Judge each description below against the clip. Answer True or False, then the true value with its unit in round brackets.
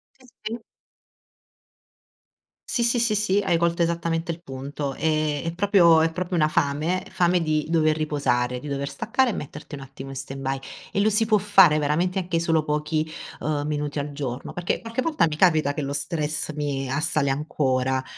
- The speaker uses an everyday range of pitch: True (3.7 semitones)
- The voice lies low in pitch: False (155 Hz)